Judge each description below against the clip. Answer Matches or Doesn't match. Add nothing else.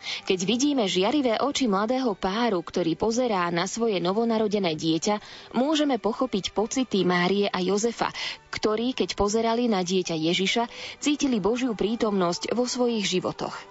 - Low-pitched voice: Doesn't match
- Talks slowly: Doesn't match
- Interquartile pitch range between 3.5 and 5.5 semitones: Matches